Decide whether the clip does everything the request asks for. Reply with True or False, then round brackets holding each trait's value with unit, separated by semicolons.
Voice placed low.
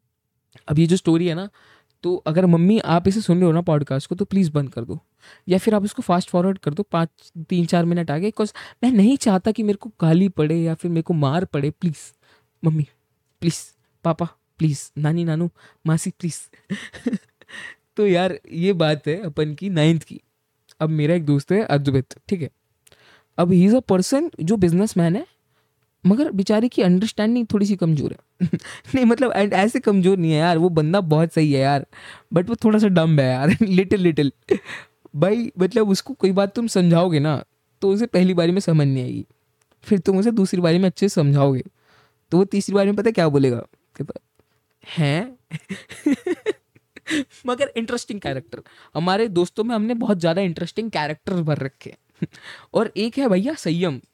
False (180 Hz)